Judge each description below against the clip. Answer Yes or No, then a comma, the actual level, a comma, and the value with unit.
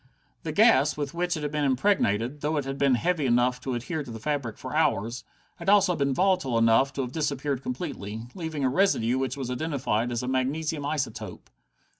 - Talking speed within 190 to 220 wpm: Yes, average, 200 wpm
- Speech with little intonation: No, average, 3.8 semitones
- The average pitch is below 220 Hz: Yes, low, 135 Hz